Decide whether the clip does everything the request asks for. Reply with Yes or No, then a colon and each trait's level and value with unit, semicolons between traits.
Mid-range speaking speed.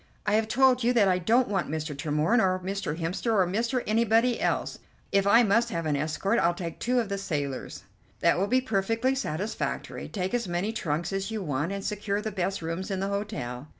No: fast, 215 wpm